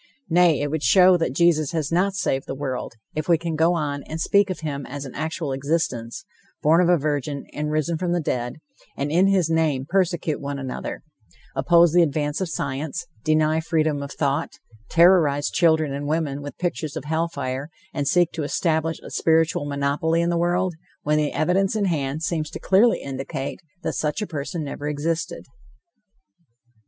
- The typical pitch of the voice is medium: Yes, medium, 155 Hz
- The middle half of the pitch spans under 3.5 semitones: Yes, average, 3.1 semitones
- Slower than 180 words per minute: No, average, 185 wpm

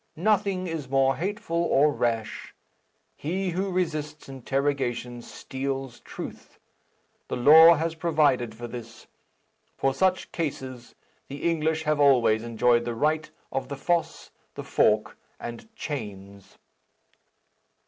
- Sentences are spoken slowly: Yes, slow, 120 wpm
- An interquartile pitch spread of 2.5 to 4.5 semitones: No, average, 5.2 semitones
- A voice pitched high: No, medium, 140 Hz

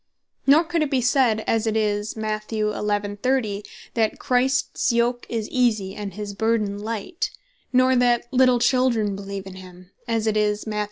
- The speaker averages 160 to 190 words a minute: Yes, average, 170 wpm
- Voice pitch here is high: Yes, high, 220 Hz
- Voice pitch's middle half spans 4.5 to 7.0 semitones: No, average, 3.2 semitones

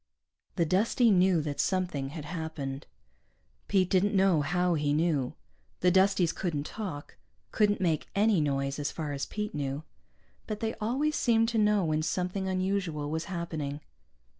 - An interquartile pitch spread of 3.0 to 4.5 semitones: No, average, 4.9 semitones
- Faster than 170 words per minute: No, average, 155 wpm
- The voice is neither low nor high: Yes, medium, 175 Hz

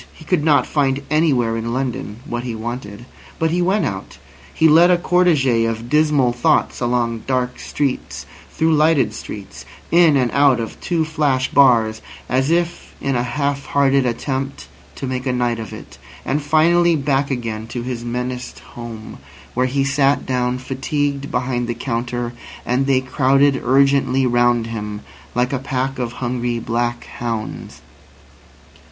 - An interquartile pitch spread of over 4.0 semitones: No, average, 2.9 semitones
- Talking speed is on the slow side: No, average, 160 wpm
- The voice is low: Yes, low, 130 Hz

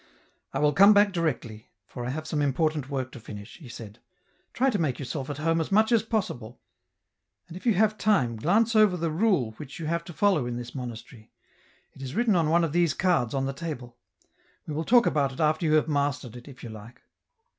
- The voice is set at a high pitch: No, medium, 155 Hz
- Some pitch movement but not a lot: No, wide, 5.9 semitones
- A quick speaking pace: Yes, fast, 235 wpm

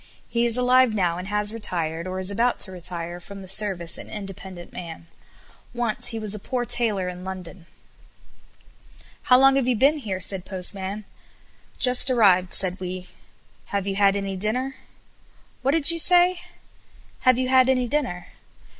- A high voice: Yes, high, 200 Hz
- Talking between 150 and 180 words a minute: Yes, average, 165 wpm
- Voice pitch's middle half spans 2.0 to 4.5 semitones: No, average, 5.2 semitones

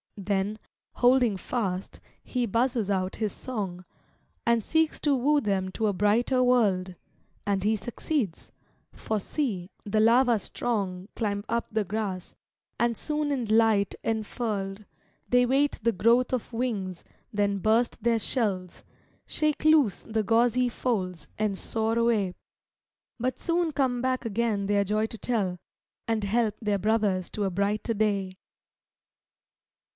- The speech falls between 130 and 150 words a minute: Yes, average, 140 wpm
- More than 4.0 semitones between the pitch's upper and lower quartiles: No, average, 3.4 semitones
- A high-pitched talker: Yes, high, 220 Hz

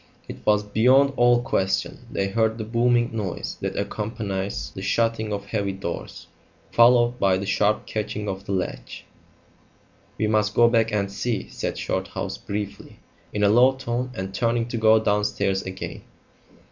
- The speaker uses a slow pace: No, average, 160 wpm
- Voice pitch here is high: No, low, 105 Hz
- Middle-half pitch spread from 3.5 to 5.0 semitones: No, average, 2.8 semitones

